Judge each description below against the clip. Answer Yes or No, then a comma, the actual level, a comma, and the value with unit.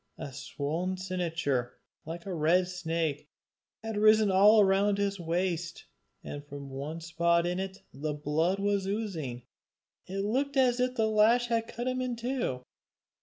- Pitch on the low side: No, medium, 185 Hz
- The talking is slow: No, average, 155 wpm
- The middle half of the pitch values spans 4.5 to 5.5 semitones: Yes, average, 5.0 semitones